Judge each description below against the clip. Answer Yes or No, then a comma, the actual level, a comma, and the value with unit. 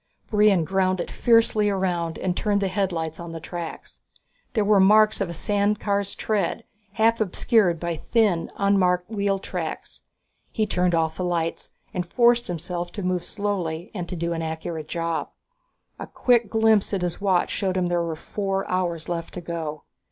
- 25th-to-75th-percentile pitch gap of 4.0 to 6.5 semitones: No, average, 3.3 semitones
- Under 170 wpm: No, average, 180 wpm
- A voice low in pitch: No, medium, 185 Hz